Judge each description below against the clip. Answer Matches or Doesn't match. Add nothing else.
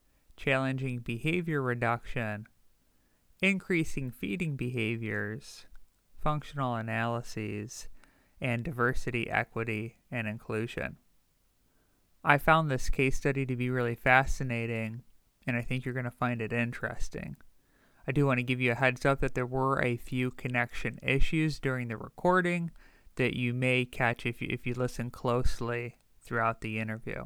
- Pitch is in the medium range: Doesn't match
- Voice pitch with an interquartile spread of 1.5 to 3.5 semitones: Matches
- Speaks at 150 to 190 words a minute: Doesn't match